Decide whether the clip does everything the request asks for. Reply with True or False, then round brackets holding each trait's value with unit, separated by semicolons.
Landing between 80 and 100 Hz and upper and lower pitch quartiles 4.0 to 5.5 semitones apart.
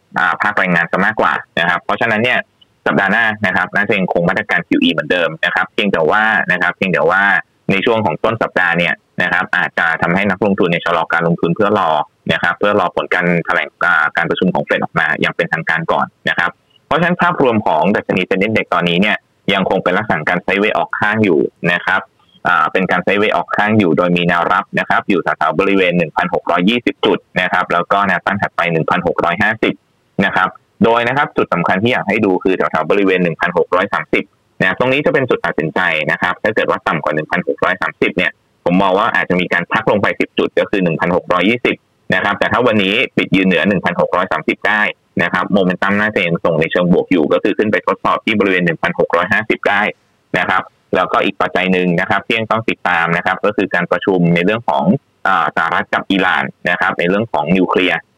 True (95 Hz; 4.3 semitones)